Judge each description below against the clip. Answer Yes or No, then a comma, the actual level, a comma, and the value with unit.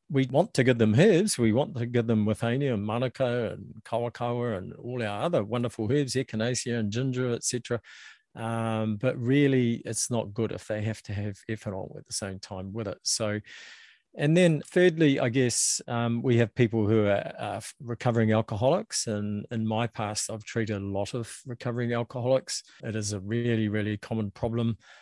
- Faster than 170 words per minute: Yes, average, 185 wpm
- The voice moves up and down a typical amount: No, narrow, 2.3 semitones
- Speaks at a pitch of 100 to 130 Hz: Yes, low, 115 Hz